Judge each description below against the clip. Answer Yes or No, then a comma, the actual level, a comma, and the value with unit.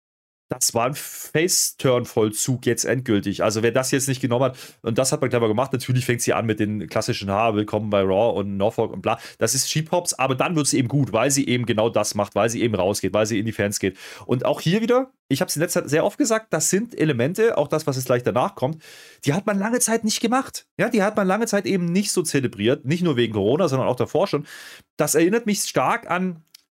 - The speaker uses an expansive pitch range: Yes, wide, 7.3 semitones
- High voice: No, low, 135 Hz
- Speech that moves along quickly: Yes, fast, 250 wpm